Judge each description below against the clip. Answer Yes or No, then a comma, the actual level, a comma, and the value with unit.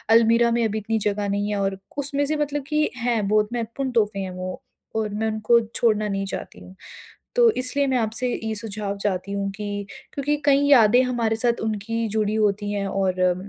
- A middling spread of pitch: Yes, average, 3.1 semitones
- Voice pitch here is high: Yes, high, 220 Hz